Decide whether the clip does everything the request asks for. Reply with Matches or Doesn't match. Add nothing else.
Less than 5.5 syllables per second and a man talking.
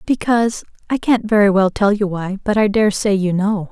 Doesn't match